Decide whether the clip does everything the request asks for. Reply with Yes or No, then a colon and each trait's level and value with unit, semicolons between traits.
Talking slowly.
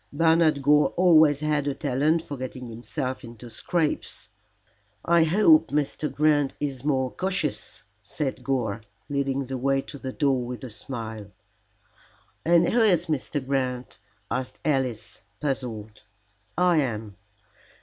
Yes: slow, 130 wpm